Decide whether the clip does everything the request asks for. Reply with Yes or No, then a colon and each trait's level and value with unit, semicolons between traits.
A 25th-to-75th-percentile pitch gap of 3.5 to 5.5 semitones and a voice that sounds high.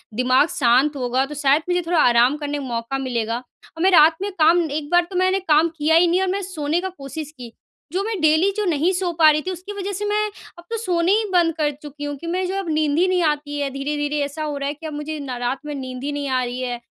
Yes: average, 4.2 semitones; very high, 300 Hz